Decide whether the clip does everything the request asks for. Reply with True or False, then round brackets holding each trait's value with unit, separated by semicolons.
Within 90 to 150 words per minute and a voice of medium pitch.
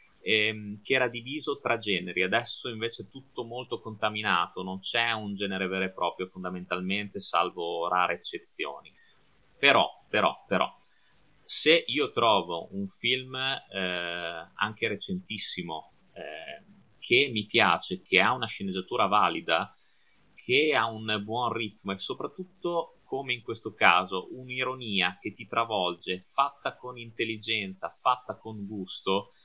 False (130 wpm; 110 Hz)